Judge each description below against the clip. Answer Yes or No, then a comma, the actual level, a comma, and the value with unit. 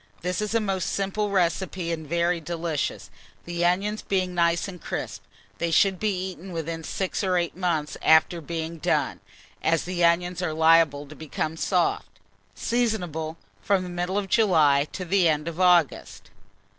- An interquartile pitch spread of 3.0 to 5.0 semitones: No, narrow, 2.6 semitones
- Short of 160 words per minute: No, average, 165 wpm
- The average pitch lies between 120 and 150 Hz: No, medium, 175 Hz